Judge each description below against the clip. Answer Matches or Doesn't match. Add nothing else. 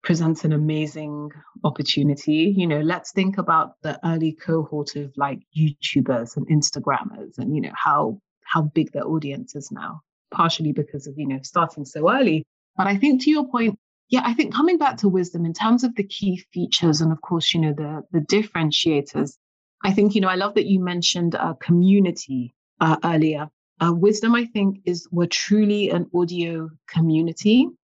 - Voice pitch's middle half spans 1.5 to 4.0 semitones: Doesn't match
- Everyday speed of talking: Matches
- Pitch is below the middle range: Doesn't match